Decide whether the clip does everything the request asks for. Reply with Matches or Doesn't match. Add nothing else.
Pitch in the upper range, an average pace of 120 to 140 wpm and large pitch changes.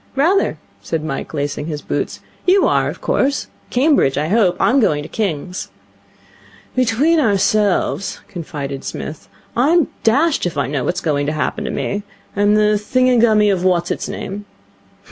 Doesn't match